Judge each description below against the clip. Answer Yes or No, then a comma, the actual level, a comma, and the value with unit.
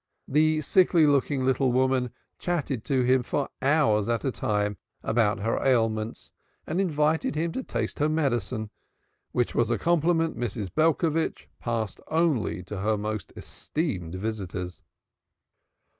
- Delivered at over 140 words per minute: No, slow, 135 wpm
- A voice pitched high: No, low, 130 Hz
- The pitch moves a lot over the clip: Yes, wide, 6.1 semitones